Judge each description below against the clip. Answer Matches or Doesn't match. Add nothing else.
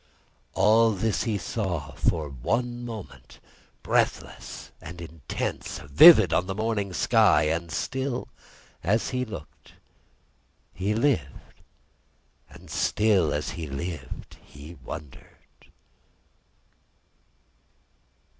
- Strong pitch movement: Matches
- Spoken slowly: Matches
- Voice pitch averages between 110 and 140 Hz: Doesn't match